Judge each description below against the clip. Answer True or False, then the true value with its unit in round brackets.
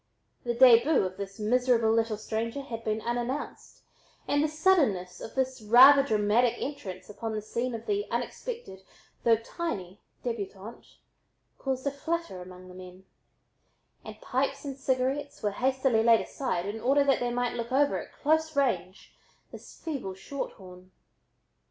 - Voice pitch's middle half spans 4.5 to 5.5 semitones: True (4.9 semitones)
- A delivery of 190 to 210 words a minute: False (155 wpm)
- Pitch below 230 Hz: False (240 Hz)